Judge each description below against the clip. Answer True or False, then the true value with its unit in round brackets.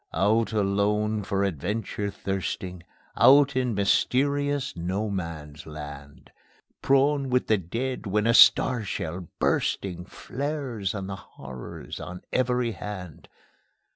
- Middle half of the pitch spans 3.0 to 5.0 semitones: False (5.4 semitones)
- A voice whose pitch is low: True (105 Hz)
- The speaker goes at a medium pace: False (115 wpm)